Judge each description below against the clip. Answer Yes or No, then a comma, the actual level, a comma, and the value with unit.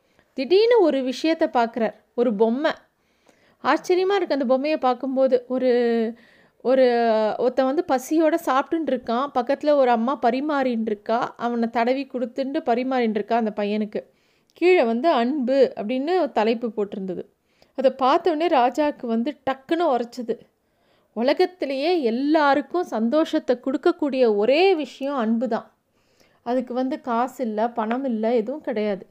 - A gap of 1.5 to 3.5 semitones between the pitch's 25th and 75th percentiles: No, average, 4.0 semitones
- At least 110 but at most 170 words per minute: Yes, average, 120 wpm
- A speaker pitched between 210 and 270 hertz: Yes, very high, 255 Hz